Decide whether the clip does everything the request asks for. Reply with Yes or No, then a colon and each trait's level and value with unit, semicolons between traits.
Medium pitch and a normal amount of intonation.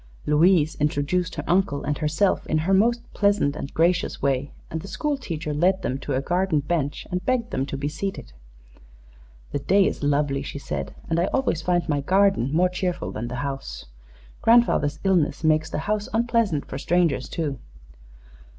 Yes: medium, 160 Hz; average, 5.0 semitones